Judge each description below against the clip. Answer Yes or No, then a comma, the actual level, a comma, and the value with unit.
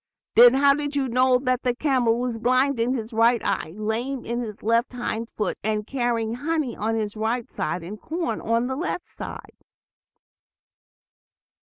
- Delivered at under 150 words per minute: No, average, 170 wpm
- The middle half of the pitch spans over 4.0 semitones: No, average, 2.7 semitones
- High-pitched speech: Yes, high, 240 Hz